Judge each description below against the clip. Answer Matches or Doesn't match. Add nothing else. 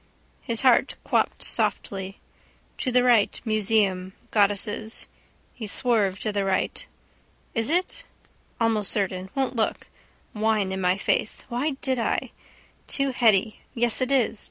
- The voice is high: Matches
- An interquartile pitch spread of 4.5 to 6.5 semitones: Doesn't match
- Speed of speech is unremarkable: Doesn't match